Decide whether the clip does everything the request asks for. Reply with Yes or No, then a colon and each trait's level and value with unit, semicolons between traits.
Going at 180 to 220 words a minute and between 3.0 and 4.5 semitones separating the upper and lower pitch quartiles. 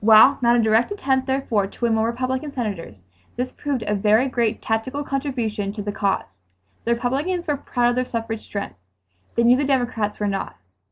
Yes: average, 190 wpm; average, 3.6 semitones